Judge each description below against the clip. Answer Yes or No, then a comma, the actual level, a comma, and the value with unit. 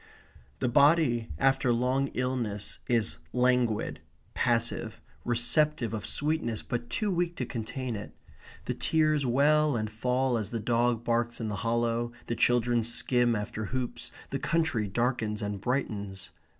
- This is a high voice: No, low, 120 Hz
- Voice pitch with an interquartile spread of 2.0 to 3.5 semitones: Yes, narrow, 2.5 semitones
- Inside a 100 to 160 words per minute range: Yes, average, 140 wpm